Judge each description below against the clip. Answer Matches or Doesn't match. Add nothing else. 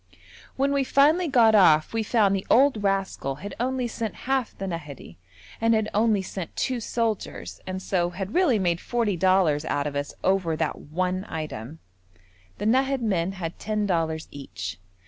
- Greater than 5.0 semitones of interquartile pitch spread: Matches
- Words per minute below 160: Doesn't match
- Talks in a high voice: Matches